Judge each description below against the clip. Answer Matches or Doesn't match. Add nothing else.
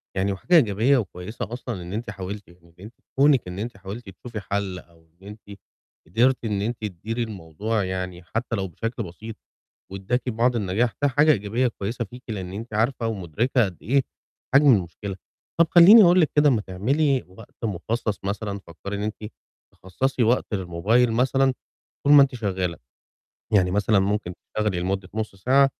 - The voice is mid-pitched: Doesn't match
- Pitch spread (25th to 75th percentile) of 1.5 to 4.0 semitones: Doesn't match